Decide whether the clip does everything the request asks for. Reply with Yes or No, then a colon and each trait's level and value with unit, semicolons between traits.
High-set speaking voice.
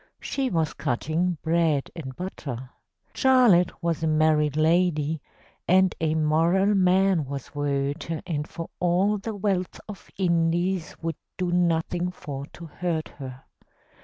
No: medium, 165 Hz